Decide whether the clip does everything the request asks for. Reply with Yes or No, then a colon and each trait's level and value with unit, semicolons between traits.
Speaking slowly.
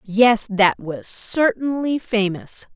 Yes: slow, 110 wpm